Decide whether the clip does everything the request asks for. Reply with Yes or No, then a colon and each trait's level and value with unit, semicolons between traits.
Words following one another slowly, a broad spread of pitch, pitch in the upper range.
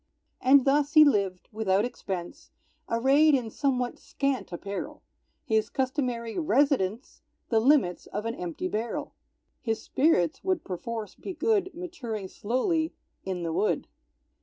Yes: slow, 130 wpm; wide, 5.8 semitones; high, 245 Hz